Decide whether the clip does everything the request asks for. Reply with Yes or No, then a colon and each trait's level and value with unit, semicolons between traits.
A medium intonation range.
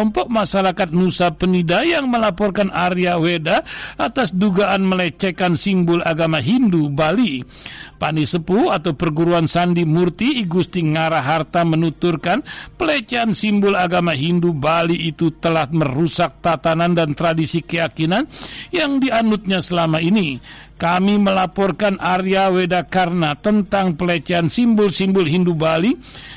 Yes: average, 3.1 semitones